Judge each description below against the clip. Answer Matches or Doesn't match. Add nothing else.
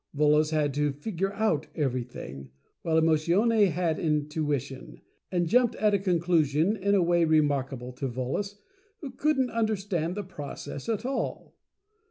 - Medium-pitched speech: Matches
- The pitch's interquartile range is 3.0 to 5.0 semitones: Doesn't match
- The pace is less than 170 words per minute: Matches